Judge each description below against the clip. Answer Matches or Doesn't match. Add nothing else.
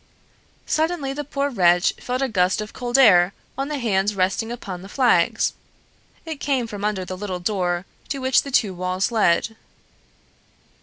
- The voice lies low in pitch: Doesn't match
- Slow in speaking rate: Doesn't match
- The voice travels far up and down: Matches